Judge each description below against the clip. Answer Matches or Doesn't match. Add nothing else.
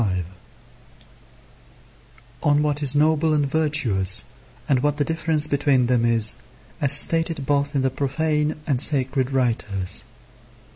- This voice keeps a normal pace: Doesn't match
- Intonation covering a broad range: Doesn't match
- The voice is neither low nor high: Matches